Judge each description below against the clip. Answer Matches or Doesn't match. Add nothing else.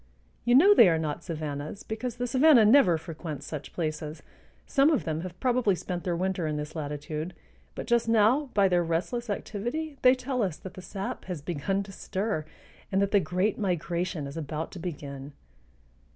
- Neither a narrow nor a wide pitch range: Doesn't match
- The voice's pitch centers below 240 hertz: Matches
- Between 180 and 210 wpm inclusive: Matches